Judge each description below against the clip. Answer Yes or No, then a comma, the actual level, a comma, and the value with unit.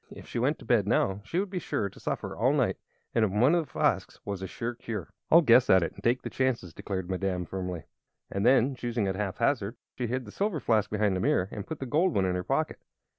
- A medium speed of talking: No, fast, 255 wpm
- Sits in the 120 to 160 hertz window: No, low, 110 Hz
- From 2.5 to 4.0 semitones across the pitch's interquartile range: No, average, 5.1 semitones